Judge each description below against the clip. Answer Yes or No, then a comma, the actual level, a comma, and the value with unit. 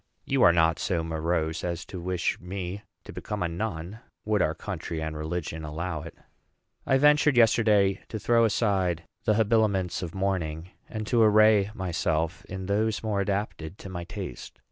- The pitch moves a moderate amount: Yes, average, 4.3 semitones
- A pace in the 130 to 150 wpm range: No, average, 165 wpm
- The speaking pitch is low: Yes, very low, 95 Hz